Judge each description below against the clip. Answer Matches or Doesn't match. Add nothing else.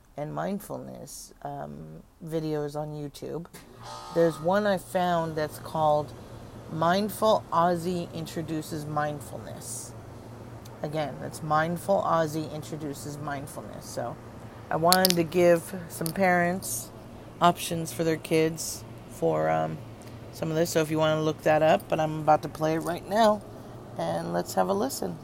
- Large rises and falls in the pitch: Matches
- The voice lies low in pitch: Doesn't match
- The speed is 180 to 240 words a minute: Doesn't match